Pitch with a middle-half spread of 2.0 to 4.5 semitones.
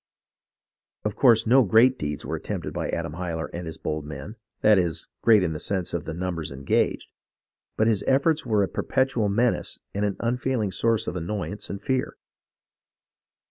No: wide, 5.5 semitones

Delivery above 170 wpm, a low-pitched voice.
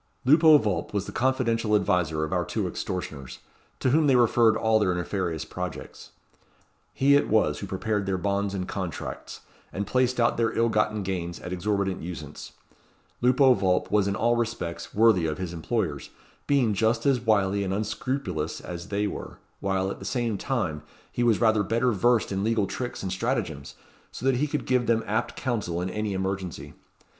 Yes: average, 180 wpm; low, 105 Hz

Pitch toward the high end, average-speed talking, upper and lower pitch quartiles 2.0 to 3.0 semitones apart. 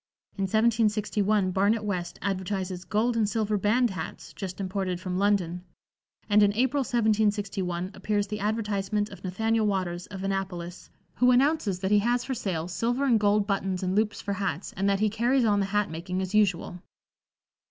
Yes: high, 205 Hz; average, 175 wpm; narrow, 2.5 semitones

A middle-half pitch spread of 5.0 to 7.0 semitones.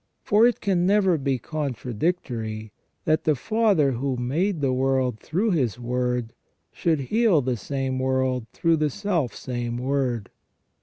Yes: average, 5.3 semitones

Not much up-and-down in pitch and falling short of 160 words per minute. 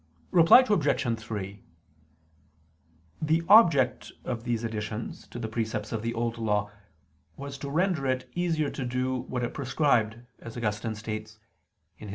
No: average, 4.1 semitones; average, 150 wpm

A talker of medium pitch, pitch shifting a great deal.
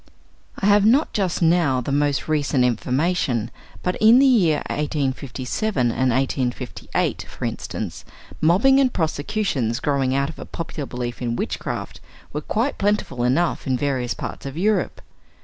Yes: medium, 145 Hz; wide, 6.9 semitones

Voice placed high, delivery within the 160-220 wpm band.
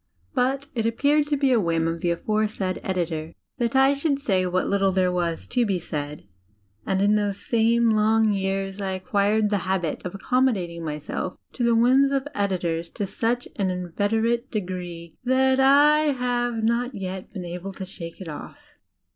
Yes: high, 205 Hz; average, 175 wpm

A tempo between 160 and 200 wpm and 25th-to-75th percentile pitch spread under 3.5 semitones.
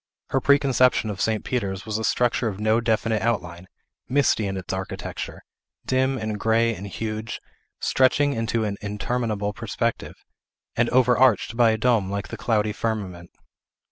No: average, 150 wpm; average, 2.9 semitones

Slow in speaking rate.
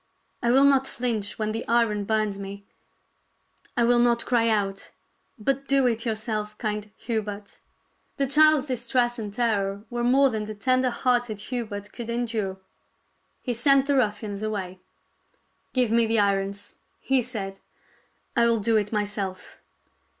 No: average, 155 wpm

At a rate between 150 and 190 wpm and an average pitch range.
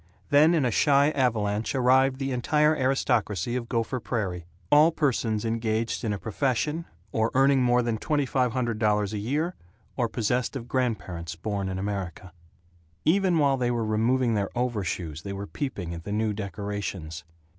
Yes: average, 165 wpm; average, 4.5 semitones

